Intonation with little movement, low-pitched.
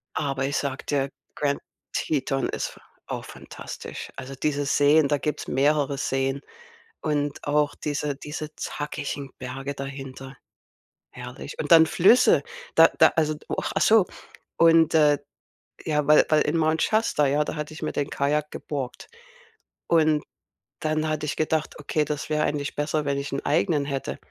No: narrow, 1.7 semitones; medium, 150 Hz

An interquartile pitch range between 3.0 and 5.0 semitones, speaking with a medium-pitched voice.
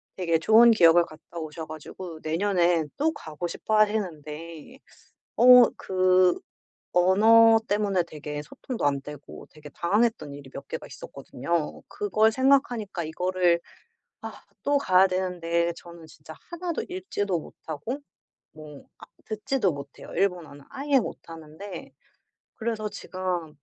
No: wide, 5.6 semitones; medium, 180 Hz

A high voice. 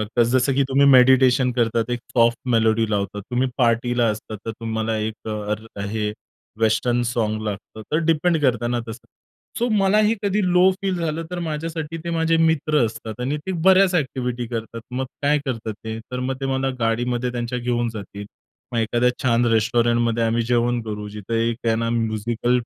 No: low, 120 Hz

